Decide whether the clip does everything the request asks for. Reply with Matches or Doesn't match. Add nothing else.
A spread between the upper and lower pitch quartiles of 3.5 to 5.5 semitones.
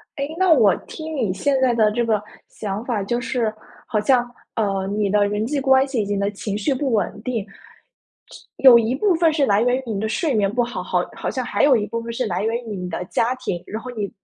Matches